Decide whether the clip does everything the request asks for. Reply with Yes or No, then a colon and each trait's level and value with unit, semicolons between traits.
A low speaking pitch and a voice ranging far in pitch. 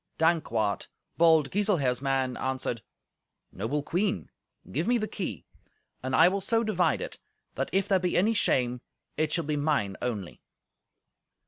No: medium, 155 Hz; wide, 6.9 semitones